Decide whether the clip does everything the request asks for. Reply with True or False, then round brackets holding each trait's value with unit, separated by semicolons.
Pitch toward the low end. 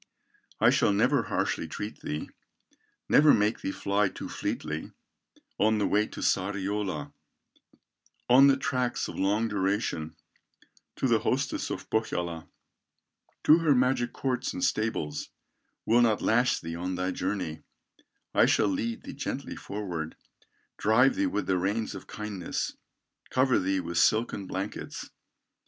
True (105 Hz)